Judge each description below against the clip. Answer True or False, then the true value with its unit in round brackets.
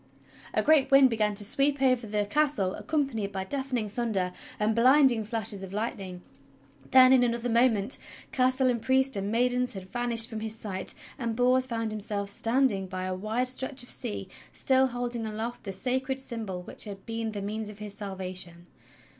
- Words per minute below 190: True (180 wpm)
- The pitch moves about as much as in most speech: True (3.9 semitones)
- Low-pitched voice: False (225 Hz)